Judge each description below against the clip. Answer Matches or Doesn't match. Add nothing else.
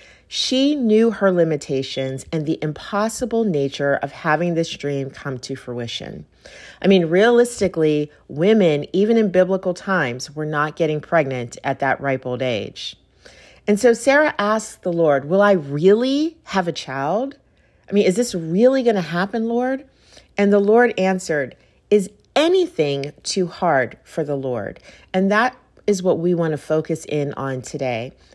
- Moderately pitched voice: Matches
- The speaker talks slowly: Doesn't match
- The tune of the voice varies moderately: Doesn't match